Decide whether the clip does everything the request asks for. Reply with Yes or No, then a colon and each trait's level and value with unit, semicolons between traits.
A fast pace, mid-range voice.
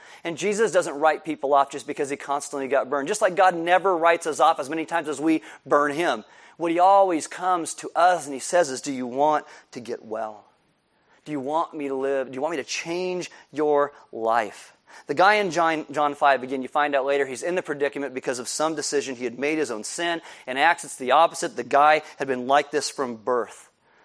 Yes: fast, 235 wpm; medium, 150 Hz